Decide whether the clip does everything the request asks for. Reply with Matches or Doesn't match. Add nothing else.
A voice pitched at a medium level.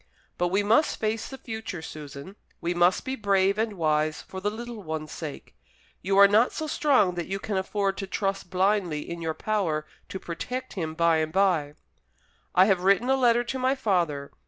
Doesn't match